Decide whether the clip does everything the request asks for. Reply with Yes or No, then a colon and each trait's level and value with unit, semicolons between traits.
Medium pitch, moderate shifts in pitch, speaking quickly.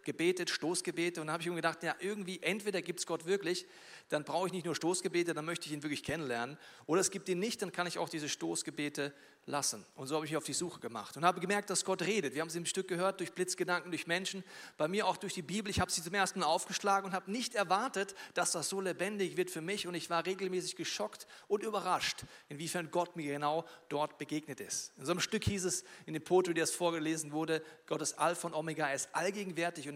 Yes: medium, 175 Hz; average, 3.3 semitones; fast, 245 wpm